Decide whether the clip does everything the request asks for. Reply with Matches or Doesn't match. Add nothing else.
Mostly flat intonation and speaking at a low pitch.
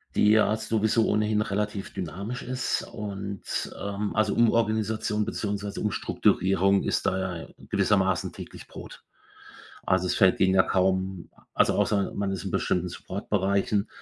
Matches